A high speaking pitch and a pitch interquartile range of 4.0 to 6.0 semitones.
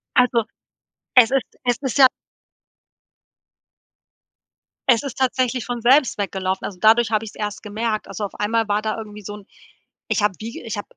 No: high, 225 Hz; average, 2.8 semitones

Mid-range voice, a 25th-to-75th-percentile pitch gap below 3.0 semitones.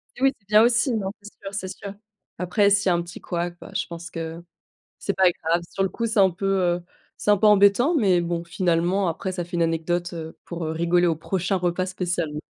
Yes: medium, 180 Hz; narrow, 2.6 semitones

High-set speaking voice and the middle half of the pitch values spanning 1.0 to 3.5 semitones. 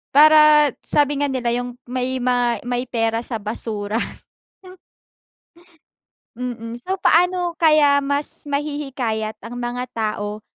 No: very high, 250 Hz; average, 4.0 semitones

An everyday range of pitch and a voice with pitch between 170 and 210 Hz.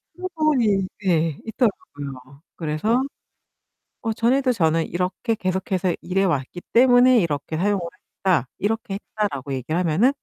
No: wide, 6.2 semitones; high, 190 Hz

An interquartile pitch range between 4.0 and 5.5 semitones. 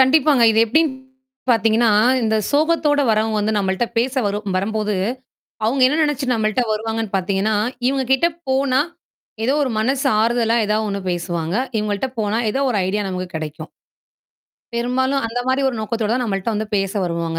Yes: average, 4.4 semitones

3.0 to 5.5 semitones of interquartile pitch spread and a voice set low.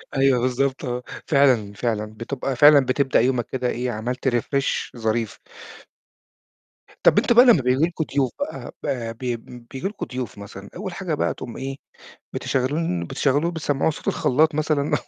Yes: average, 3.4 semitones; low, 130 Hz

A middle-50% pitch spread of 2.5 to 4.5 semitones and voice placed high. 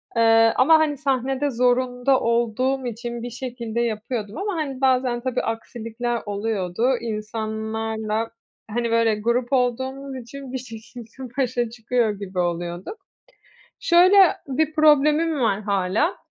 Yes: average, 3.1 semitones; high, 240 Hz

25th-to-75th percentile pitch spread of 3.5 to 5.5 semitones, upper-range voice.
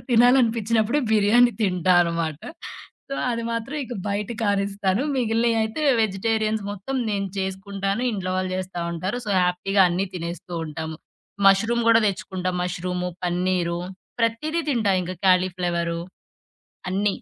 Yes: average, 3.8 semitones; high, 195 Hz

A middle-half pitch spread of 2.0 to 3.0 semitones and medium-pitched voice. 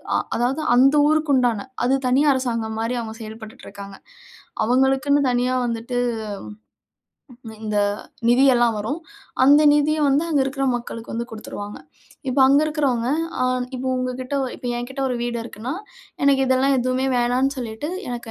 No: narrow, 2.6 semitones; very high, 250 Hz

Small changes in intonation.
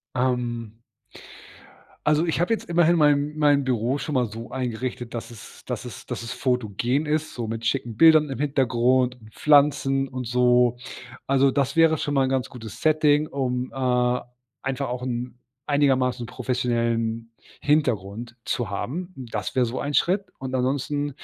No: average, 3.1 semitones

